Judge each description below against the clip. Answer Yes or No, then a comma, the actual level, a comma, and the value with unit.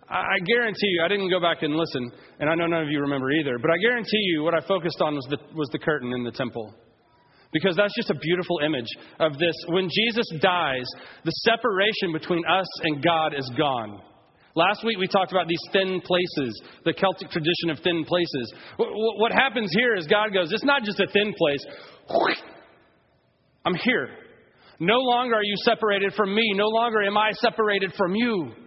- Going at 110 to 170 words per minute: No, average, 195 wpm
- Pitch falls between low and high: Yes, medium, 180 Hz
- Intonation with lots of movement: No, average, 4.8 semitones